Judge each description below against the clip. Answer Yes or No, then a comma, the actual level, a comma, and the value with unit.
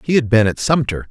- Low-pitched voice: Yes, low, 120 Hz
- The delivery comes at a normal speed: No, fast, 270 wpm